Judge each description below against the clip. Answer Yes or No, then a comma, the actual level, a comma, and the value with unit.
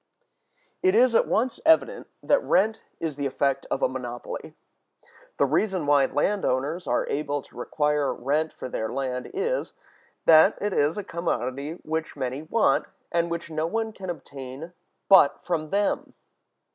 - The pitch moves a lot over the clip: Yes, wide, 6.6 semitones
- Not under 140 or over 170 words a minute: Yes, average, 160 wpm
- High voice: No, medium, 160 Hz